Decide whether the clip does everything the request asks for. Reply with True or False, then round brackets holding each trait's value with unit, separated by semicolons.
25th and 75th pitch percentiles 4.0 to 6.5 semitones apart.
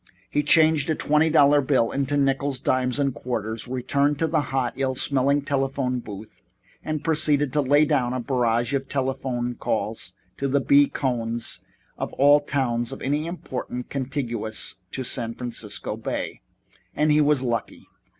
False (2.8 semitones)